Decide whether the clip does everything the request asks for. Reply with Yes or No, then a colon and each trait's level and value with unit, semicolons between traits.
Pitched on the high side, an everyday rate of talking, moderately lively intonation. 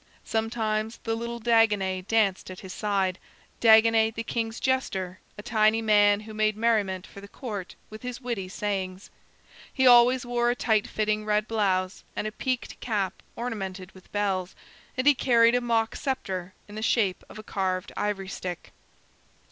Yes: high, 215 Hz; average, 165 wpm; average, 3.1 semitones